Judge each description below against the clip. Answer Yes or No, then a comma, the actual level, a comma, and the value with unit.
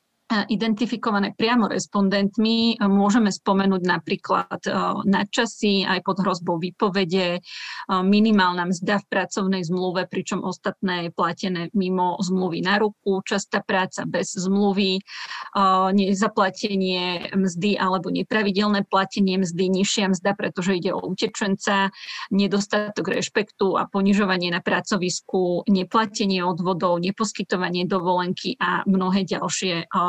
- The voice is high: Yes, high, 195 Hz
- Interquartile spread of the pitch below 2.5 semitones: Yes, narrow, 1.8 semitones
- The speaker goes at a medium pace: No, slow, 105 wpm